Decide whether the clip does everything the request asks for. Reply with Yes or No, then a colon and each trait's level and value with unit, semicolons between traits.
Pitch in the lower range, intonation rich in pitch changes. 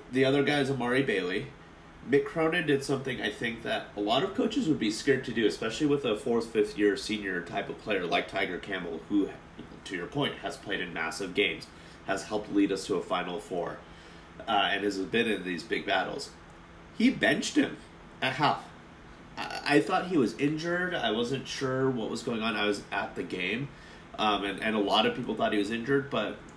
Yes: low, 115 Hz; wide, 6.5 semitones